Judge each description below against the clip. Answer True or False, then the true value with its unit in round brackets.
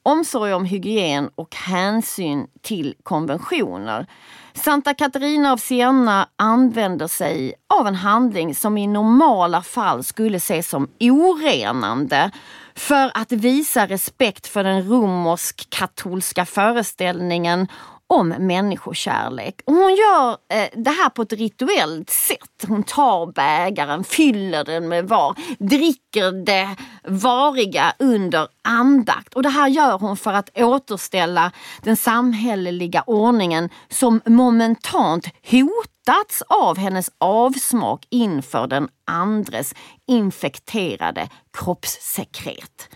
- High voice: True (215 Hz)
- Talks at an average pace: False (110 wpm)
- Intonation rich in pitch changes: True (5.9 semitones)